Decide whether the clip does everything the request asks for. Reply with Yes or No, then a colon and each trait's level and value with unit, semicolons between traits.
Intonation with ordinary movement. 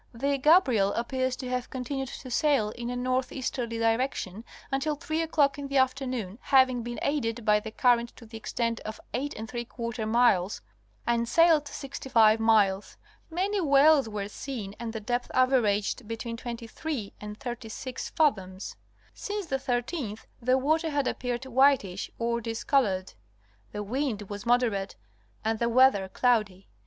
Yes: average, 3.5 semitones